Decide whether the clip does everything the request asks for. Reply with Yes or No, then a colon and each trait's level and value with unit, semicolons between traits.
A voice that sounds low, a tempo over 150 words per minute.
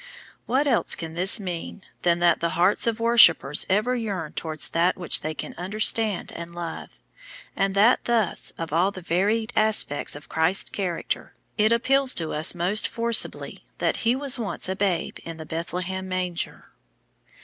No: medium, 185 Hz; average, 165 wpm